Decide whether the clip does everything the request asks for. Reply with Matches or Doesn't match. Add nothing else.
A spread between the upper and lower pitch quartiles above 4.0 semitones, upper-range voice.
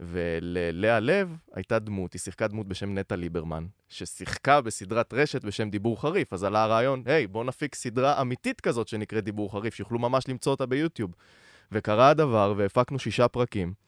Doesn't match